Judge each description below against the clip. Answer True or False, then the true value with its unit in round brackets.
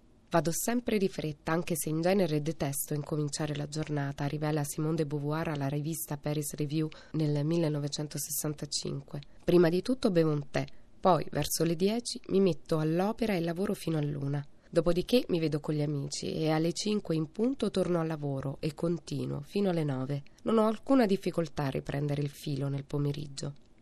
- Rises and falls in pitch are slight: False (3.0 semitones)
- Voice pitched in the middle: True (155 Hz)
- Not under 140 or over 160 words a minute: False (170 wpm)